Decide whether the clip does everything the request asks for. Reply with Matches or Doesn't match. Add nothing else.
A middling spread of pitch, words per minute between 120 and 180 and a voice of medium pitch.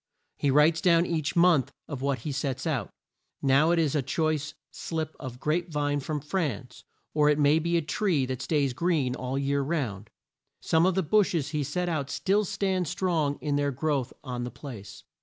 Doesn't match